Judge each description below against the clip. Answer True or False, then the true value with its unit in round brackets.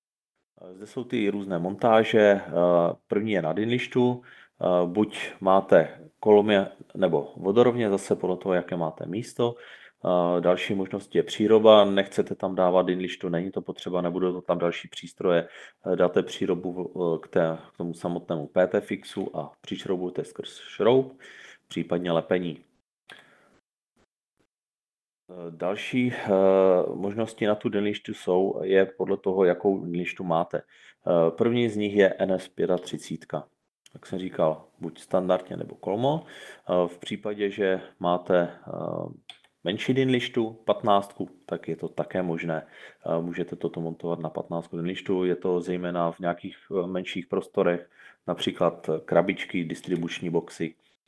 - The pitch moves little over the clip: False (3.0 semitones)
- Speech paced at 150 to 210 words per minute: False (120 wpm)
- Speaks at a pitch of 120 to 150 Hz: False (90 Hz)